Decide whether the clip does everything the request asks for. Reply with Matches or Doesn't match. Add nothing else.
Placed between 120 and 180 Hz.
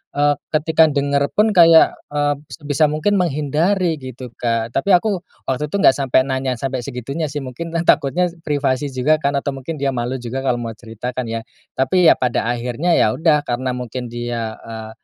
Matches